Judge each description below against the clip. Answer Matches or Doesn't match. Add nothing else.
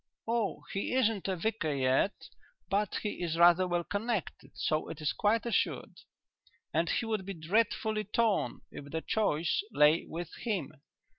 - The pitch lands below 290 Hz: Matches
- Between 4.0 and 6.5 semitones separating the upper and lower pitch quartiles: Matches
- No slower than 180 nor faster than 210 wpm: Doesn't match